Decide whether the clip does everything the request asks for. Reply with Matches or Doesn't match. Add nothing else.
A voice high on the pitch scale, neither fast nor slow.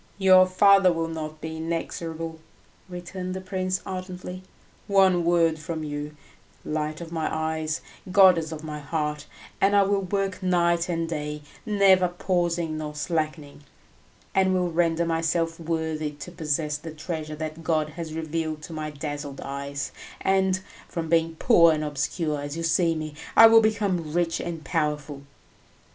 Doesn't match